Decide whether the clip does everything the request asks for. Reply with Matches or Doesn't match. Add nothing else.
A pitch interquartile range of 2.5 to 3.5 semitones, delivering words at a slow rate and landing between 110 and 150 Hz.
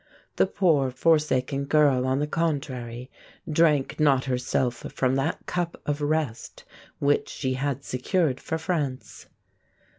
Matches